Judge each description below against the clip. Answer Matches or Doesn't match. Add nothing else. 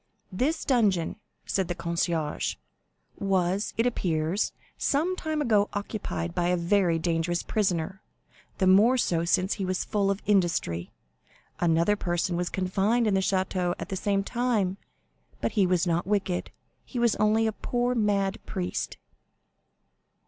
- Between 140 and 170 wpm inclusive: Matches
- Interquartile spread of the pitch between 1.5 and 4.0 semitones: Matches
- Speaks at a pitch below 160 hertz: Doesn't match